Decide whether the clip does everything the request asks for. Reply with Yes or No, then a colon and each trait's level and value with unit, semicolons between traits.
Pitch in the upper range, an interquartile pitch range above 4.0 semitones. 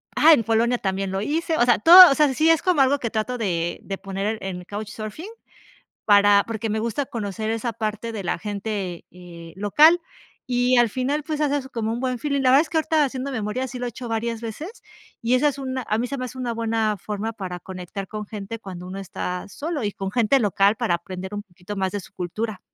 Yes: high, 225 Hz; average, 4.5 semitones